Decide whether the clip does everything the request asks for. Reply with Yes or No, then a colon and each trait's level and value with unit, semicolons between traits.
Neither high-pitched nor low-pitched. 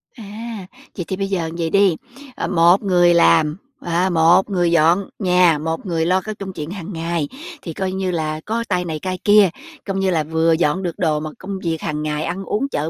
Yes: medium, 175 Hz